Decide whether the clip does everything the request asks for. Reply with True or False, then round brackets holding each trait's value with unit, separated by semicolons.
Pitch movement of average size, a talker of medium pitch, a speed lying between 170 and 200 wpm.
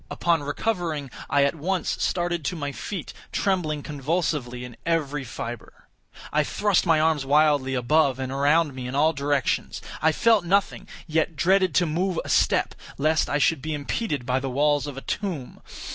True (3.4 semitones; 150 Hz; 175 wpm)